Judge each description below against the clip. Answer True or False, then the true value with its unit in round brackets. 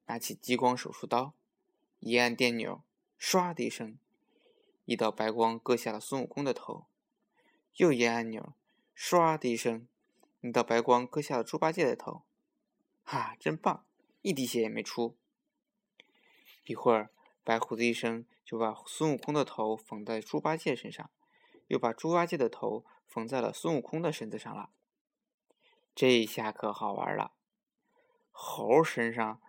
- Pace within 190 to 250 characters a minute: True (215 characters per minute)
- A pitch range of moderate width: False (6.7 semitones)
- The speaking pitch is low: True (125 Hz)